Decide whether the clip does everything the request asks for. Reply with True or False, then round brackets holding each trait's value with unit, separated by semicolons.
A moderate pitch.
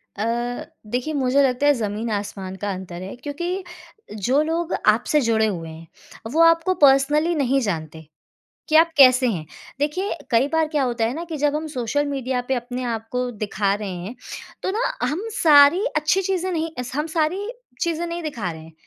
False (270 Hz)